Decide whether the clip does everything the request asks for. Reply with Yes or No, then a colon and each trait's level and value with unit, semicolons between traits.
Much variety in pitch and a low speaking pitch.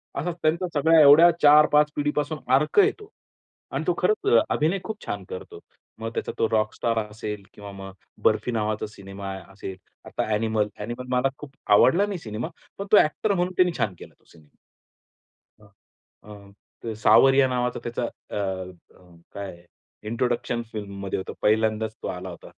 Yes: wide, 6.3 semitones; low, 120 Hz